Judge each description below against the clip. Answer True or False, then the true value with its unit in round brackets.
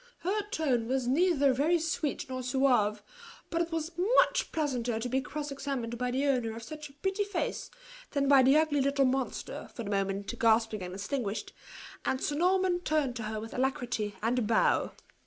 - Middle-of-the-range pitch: False (265 Hz)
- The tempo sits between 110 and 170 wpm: False (190 wpm)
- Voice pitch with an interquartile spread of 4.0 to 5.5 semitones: True (5.0 semitones)